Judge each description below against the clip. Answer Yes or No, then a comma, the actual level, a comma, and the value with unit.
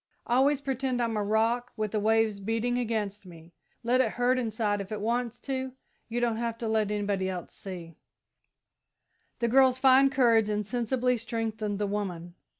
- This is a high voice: Yes, high, 225 Hz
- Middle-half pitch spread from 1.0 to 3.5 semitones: Yes, average, 2.9 semitones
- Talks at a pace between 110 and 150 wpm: No, average, 165 wpm